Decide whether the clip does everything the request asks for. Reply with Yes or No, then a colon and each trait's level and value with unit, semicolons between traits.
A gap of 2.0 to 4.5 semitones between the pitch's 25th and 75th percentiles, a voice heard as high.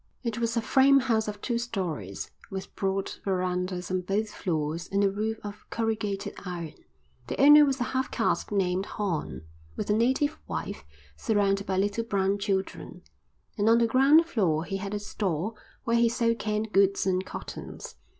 Yes: average, 3.4 semitones; high, 205 Hz